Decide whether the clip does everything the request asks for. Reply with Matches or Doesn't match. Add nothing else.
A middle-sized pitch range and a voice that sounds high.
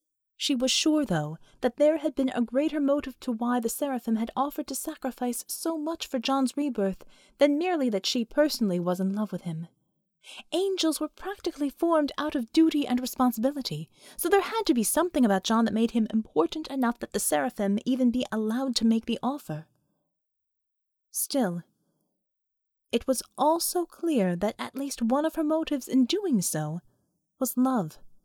Doesn't match